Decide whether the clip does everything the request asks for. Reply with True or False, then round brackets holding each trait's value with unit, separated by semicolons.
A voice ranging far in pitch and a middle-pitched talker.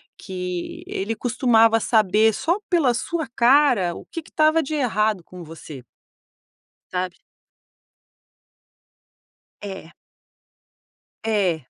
False (6.3 semitones; 220 Hz)